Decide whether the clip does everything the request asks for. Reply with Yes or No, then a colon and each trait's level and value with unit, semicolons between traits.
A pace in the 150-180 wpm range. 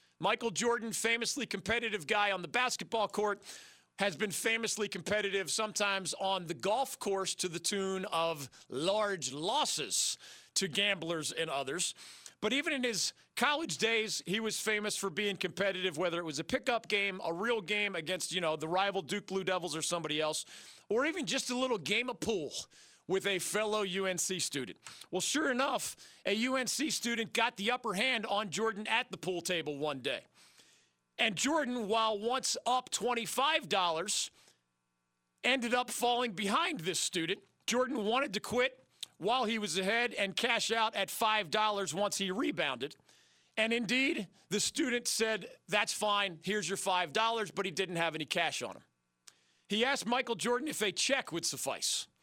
Yes: average, 170 wpm